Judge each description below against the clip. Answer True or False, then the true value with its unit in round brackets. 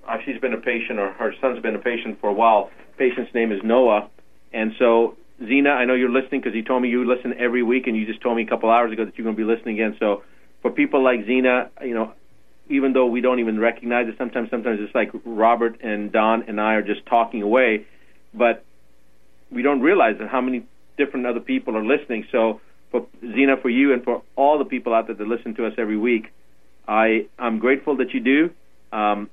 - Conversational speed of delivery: False (230 wpm)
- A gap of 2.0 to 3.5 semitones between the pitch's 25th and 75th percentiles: True (2.6 semitones)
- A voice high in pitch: False (115 Hz)